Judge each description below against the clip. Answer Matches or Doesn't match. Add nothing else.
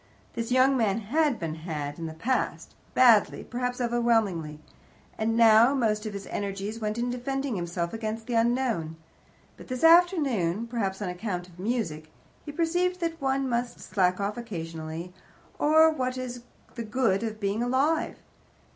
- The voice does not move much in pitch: Doesn't match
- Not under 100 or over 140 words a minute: Doesn't match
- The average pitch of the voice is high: Matches